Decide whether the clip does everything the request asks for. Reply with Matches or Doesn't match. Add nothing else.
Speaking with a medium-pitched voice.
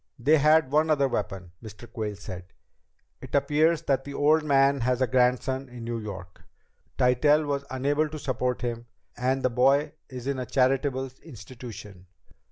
Doesn't match